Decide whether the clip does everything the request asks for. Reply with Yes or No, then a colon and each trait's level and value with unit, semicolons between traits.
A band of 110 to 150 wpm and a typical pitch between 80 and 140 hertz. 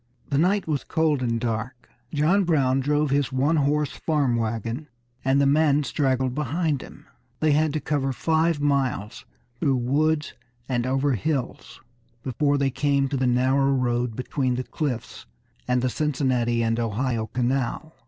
No: average, 160 wpm; low, 135 Hz